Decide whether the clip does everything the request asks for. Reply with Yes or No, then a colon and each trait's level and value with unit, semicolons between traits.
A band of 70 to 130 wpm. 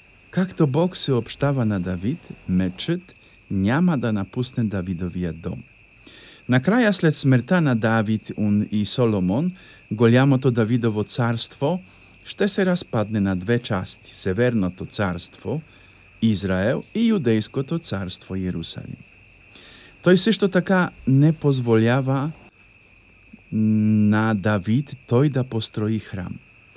Yes: slow, 110 wpm